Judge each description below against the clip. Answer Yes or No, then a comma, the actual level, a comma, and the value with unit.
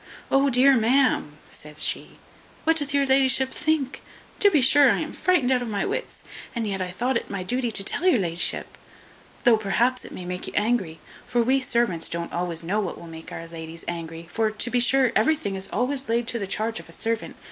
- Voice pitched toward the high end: Yes, high, 230 Hz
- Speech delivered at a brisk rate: Yes, fast, 220 wpm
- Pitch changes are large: Yes, wide, 6.3 semitones